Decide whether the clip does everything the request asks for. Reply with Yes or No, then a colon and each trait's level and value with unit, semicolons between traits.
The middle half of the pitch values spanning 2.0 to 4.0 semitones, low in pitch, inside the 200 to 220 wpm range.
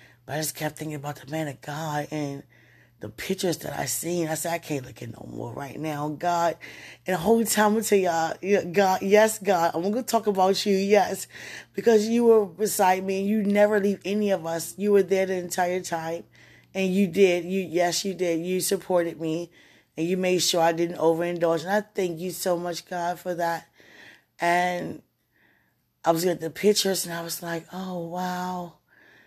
No: average, 2.8 semitones; medium, 180 Hz; fast, 205 wpm